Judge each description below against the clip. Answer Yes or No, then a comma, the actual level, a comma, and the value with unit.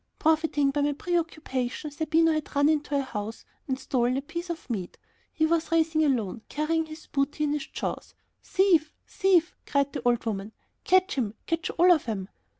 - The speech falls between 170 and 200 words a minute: Yes, average, 180 wpm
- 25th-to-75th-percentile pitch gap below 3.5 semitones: No, average, 3.8 semitones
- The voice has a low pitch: No, very high, 300 Hz